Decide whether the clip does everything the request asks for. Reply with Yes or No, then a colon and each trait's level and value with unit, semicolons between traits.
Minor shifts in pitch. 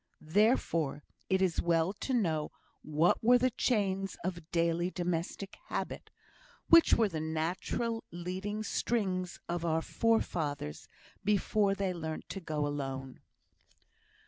No: average, 4.2 semitones